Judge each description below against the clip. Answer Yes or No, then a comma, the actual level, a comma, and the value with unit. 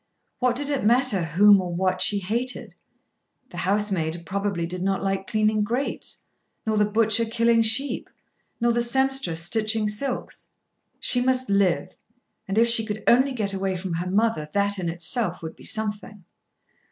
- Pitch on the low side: No, high, 210 Hz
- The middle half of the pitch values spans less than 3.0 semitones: No, average, 3.8 semitones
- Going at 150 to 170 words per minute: Yes, average, 165 wpm